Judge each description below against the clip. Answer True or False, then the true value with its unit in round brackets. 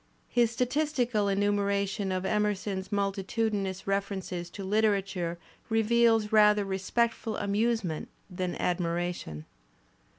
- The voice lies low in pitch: False (200 Hz)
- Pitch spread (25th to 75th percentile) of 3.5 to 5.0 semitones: False (2.6 semitones)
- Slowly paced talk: True (95 wpm)